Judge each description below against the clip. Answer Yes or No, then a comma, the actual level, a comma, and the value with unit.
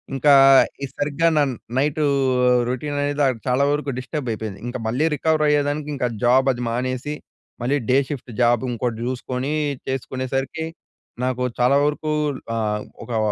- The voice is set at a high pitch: No, low, 130 Hz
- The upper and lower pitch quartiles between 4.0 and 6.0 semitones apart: No, average, 2.9 semitones